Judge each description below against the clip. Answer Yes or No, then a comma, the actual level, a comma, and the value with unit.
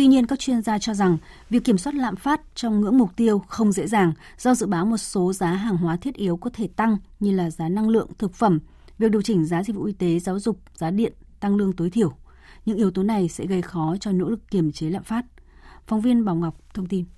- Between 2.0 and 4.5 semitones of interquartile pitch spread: Yes, average, 3.9 semitones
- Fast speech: Yes, fast, 260 wpm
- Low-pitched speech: No, high, 205 Hz